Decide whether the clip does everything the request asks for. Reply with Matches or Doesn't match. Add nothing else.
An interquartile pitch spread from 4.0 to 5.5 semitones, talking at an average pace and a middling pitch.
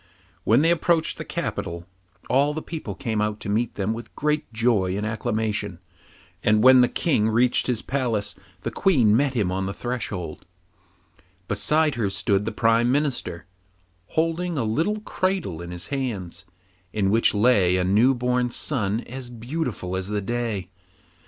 Doesn't match